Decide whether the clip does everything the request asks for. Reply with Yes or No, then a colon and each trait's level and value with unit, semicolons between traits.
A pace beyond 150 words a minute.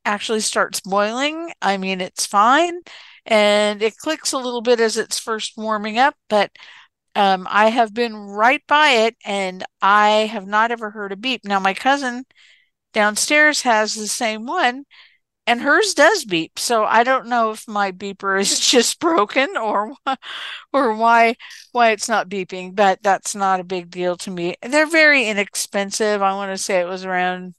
Yes: average, 175 wpm